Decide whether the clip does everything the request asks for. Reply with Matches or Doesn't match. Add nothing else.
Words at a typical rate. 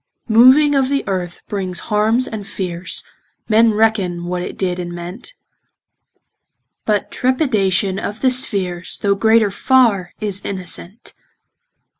Doesn't match